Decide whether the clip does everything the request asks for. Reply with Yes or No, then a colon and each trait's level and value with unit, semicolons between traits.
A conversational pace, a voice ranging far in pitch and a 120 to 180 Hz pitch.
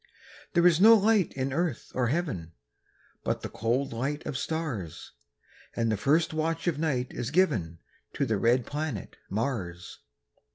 Yes: average, 155 wpm; wide, 6.1 semitones; medium, 140 Hz